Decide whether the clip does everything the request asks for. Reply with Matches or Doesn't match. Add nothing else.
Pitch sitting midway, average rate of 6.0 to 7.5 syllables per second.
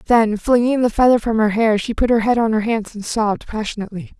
Doesn't match